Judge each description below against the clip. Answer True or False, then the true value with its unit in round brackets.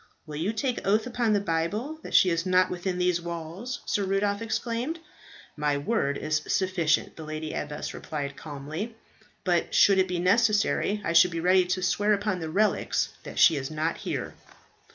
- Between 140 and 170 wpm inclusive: False (180 wpm)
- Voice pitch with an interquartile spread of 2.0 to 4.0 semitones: False (4.5 semitones)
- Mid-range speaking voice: True (180 Hz)